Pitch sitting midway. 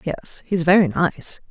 Yes: medium, 170 Hz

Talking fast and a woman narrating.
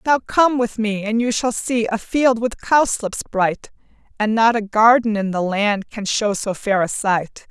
Yes: fast, 210 wpm; female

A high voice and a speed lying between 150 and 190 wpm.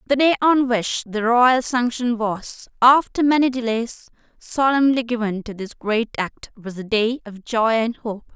Yes: high, 235 Hz; average, 170 wpm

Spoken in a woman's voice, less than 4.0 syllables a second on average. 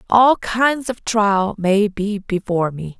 Yes: female; 3.6 syllables/s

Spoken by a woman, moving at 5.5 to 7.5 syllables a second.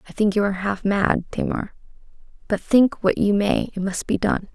No: female; 5.2 syllables/s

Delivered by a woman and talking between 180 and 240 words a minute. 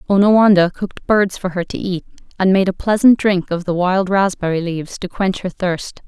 Yes: female; fast, 205 wpm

